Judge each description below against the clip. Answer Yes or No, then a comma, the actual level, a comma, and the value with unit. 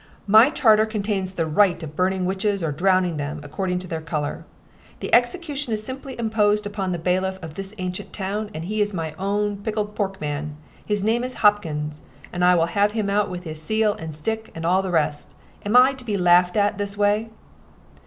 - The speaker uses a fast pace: Yes, fast, 210 wpm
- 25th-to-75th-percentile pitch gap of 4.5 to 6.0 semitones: No, average, 3.5 semitones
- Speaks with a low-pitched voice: No, high, 195 Hz